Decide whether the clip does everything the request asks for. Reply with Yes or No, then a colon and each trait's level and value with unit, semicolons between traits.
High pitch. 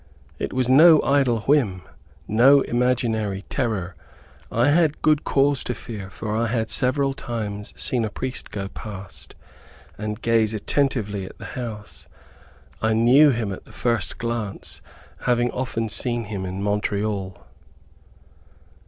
No: low, 115 Hz